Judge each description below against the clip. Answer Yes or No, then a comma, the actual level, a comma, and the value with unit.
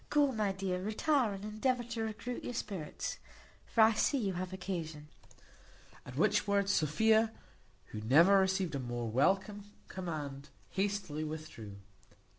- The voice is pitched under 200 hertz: Yes, high, 190 Hz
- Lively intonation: Yes, wide, 5.7 semitones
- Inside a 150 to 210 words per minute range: No, average, 140 wpm